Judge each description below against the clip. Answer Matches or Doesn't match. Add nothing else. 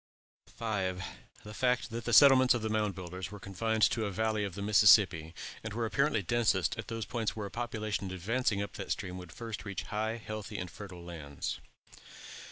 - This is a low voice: Matches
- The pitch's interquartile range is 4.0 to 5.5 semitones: Doesn't match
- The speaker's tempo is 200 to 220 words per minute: Doesn't match